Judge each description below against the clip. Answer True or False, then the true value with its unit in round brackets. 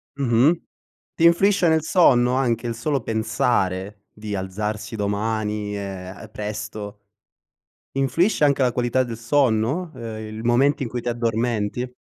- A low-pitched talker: True (115 Hz)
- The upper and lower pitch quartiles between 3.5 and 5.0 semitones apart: True (3.8 semitones)